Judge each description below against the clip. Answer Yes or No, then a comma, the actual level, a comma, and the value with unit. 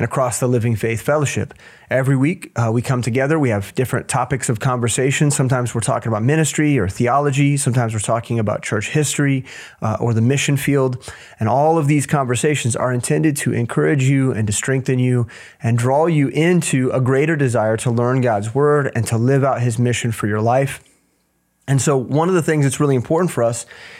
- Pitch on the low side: Yes, low, 130 Hz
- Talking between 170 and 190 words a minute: No, fast, 205 wpm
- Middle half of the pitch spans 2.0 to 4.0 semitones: Yes, average, 3.1 semitones